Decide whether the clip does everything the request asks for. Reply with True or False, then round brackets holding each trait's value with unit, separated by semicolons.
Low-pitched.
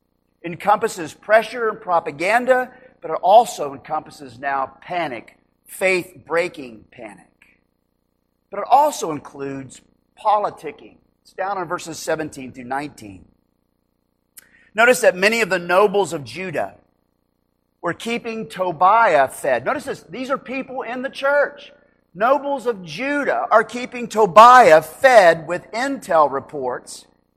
False (175 Hz)